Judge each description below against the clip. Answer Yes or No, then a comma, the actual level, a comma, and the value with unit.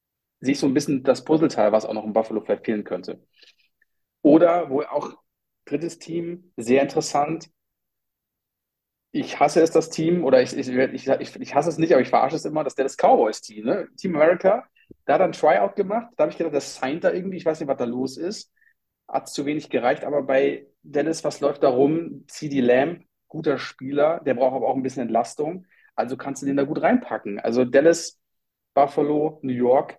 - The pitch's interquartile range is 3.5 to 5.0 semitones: Yes, average, 3.8 semitones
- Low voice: No, medium, 145 Hz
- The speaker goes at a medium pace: No, fast, 205 wpm